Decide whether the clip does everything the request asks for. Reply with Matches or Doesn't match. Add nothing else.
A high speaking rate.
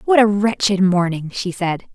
Doesn't match